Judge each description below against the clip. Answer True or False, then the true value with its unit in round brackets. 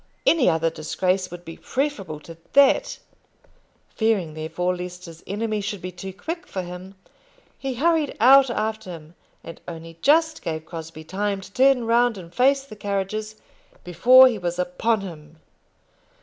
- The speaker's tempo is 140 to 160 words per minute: True (155 wpm)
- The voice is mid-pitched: False (195 Hz)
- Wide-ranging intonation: True (5.8 semitones)